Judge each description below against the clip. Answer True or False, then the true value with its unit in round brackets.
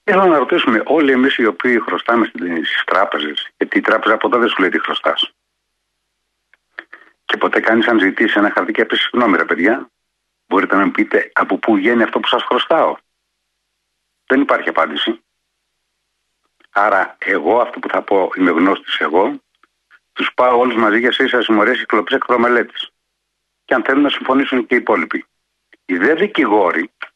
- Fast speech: False (160 wpm)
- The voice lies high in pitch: True (280 Hz)